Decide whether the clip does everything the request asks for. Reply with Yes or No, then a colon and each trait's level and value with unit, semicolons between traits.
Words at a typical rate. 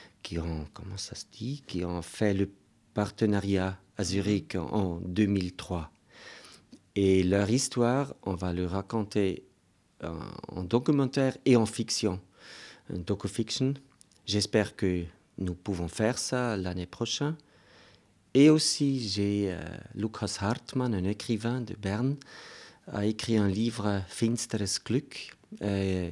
No: slow, 125 wpm